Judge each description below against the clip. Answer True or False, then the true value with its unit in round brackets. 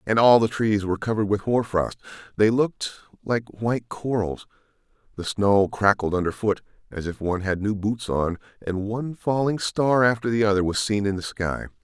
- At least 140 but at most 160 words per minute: False (195 wpm)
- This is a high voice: False (105 Hz)